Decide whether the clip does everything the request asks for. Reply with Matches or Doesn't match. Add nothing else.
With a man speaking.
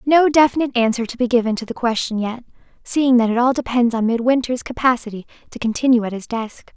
Doesn't match